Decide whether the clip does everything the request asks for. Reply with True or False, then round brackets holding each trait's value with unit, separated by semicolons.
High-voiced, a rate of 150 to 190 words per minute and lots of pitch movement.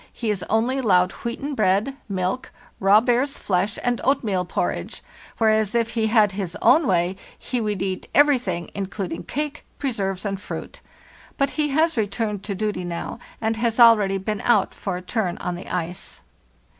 False (215 Hz; 170 wpm; 4.1 semitones)